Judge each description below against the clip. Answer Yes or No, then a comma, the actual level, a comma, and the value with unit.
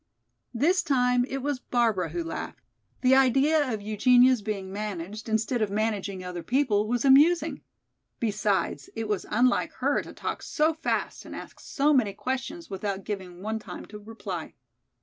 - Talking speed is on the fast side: No, average, 160 wpm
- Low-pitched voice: No, high, 220 Hz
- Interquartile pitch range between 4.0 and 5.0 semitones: Yes, average, 4.5 semitones